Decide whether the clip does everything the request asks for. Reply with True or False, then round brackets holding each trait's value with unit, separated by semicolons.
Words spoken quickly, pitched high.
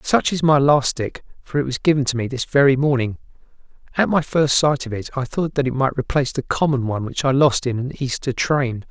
False (240 wpm; 135 Hz)